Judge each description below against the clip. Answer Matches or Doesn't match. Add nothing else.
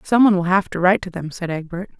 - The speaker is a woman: Matches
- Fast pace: Matches